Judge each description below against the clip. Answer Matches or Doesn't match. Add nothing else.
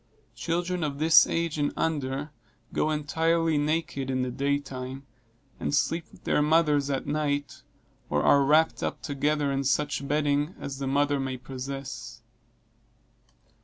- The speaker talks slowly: Doesn't match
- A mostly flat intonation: Matches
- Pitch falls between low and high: Matches